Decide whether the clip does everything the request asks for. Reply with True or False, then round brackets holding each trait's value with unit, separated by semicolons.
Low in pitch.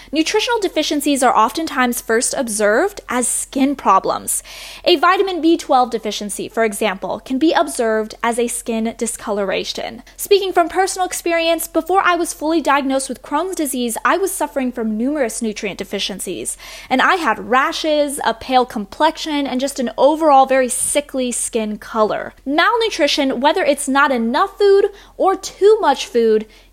False (275 Hz)